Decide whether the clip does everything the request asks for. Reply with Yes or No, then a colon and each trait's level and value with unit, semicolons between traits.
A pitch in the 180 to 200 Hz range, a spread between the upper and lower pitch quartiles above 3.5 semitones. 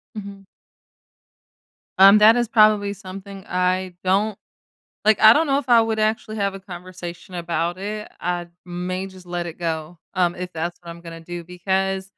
No: medium, 185 Hz; average, 3.0 semitones